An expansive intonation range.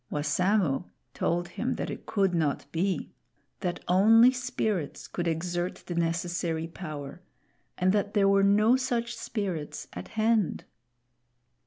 No: average, 4.1 semitones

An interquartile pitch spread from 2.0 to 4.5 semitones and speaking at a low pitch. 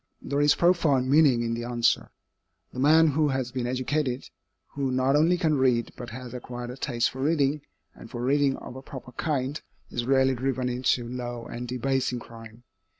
Yes: narrow, 2.6 semitones; low, 130 Hz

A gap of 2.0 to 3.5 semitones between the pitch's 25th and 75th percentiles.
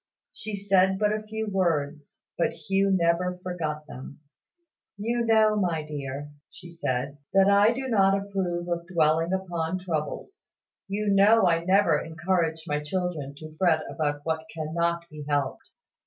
No: average, 3.9 semitones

